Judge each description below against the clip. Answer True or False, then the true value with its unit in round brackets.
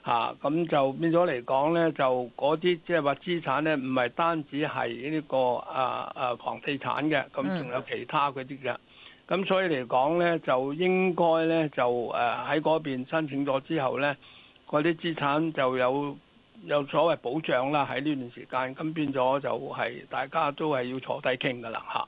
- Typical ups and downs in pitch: True (3.9 semitones)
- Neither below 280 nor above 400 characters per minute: False (260 characters per minute)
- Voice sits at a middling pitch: True (145 Hz)